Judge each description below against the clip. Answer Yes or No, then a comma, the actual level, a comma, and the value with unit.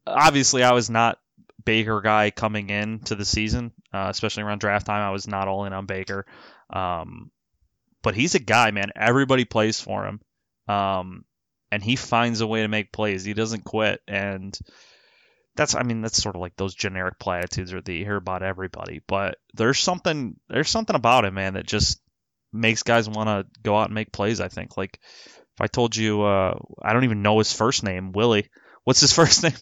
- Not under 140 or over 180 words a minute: No, average, 195 wpm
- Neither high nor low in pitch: No, low, 105 Hz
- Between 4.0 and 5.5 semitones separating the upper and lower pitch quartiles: No, average, 2.8 semitones